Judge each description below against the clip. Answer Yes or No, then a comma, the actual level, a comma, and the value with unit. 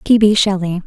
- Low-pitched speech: No, high, 195 Hz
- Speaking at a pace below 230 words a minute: Yes, fast, 210 wpm